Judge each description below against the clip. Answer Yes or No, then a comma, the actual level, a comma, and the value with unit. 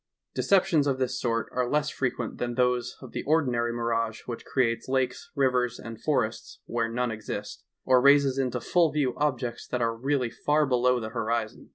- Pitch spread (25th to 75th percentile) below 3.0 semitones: Yes, narrow, 2.4 semitones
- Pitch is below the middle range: Yes, low, 125 Hz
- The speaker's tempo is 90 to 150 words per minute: No, average, 185 wpm